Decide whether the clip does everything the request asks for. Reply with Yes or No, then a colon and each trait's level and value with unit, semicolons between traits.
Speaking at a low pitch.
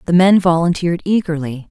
No: medium, 170 Hz